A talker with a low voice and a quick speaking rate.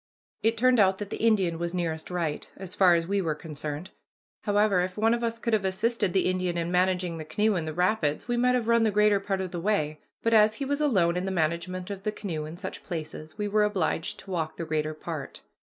No: medium, 185 Hz; fast, 245 wpm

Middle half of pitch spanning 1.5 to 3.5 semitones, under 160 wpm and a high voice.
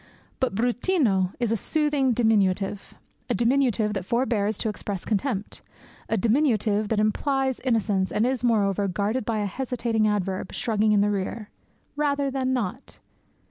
No: average, 4.0 semitones; average, 145 wpm; high, 220 Hz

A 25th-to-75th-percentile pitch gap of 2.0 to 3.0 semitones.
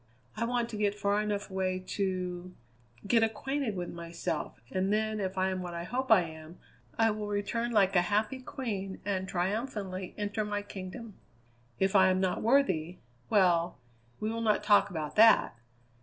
Yes: average, 2.7 semitones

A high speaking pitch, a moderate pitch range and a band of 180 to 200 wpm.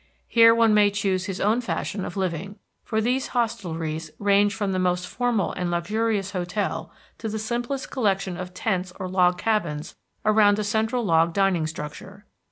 No: high, 200 Hz; average, 3.4 semitones; average, 170 wpm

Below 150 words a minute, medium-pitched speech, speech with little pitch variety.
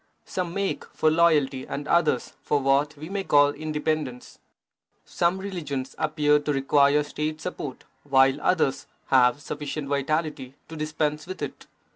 Yes: average, 140 wpm; medium, 150 Hz; narrow, 2.1 semitones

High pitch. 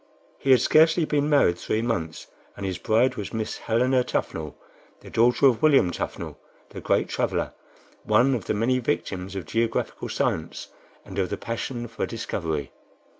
No: low, 115 Hz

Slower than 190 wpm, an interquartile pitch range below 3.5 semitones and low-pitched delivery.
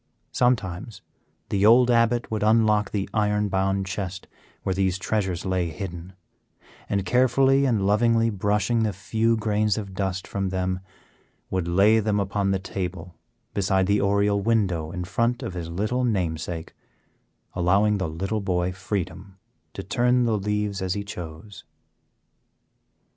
Yes: average, 140 wpm; narrow, 2.6 semitones; low, 100 Hz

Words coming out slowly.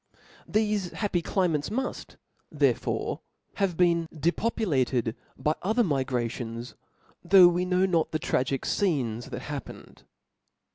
Yes: slow, 110 wpm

